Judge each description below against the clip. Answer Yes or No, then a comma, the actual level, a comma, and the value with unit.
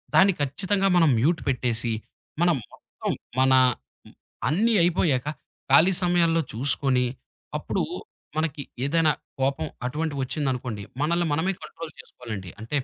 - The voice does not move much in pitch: No, average, 4.6 semitones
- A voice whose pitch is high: No, medium, 150 Hz